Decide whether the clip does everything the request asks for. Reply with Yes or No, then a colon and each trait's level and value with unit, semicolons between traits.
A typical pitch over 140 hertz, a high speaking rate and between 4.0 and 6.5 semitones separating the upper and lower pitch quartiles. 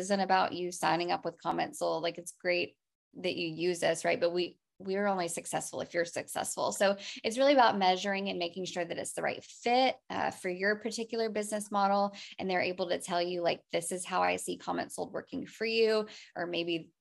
No: medium, 185 Hz; fast, 220 wpm; average, 2.9 semitones